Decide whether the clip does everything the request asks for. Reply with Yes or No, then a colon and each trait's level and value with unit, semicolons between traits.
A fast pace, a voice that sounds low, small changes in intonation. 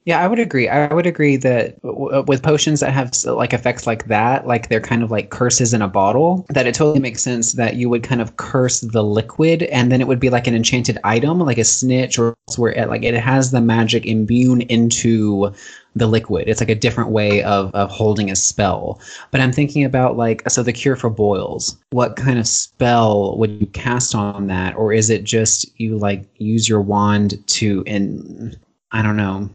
No: fast, 215 wpm; low, 115 Hz; average, 3.0 semitones